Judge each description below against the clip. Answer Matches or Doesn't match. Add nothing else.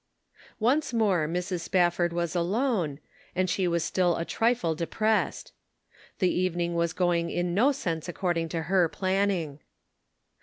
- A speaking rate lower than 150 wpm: Matches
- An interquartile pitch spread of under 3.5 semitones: Matches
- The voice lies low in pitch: Doesn't match